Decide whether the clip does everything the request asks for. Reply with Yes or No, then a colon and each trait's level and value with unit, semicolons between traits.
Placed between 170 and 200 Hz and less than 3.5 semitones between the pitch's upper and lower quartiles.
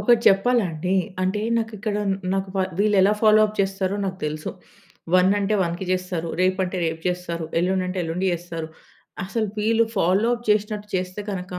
Yes: high, 190 Hz; average, 2.7 semitones